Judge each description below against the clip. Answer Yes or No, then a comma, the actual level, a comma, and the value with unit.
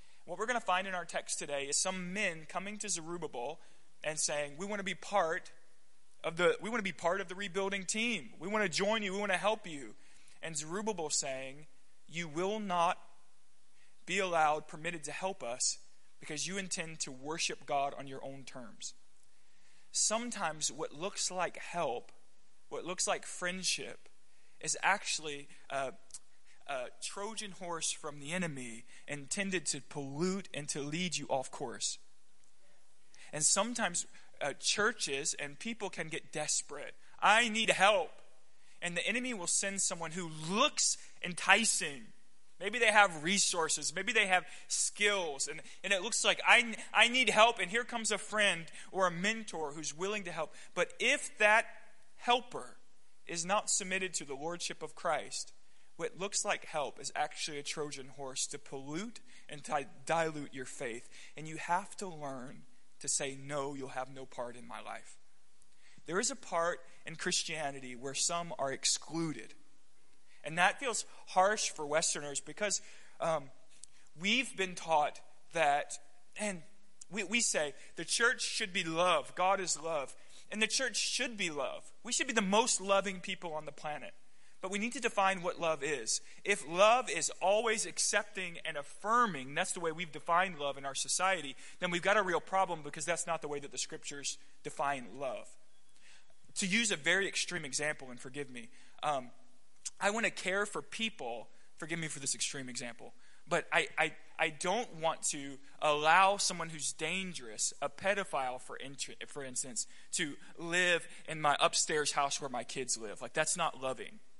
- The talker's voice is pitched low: No, medium, 175 Hz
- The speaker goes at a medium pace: Yes, average, 175 wpm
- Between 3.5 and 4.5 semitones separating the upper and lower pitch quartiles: No, average, 5.3 semitones